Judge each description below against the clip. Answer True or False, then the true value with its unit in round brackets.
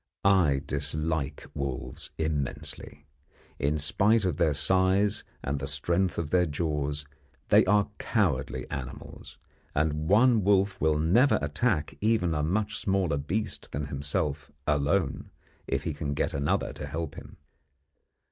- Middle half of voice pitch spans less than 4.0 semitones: False (4.9 semitones)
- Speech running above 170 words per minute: False (135 wpm)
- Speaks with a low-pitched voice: True (75 Hz)